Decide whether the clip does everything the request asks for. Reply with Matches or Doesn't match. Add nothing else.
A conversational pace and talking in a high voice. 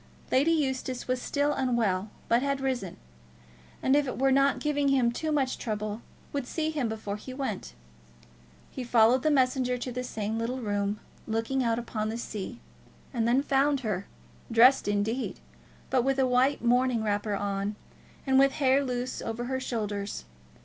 Matches